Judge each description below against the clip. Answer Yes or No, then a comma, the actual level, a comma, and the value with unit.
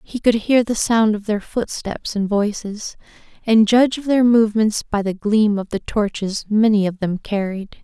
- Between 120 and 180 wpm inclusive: No, average, 190 wpm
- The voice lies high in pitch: Yes, high, 215 Hz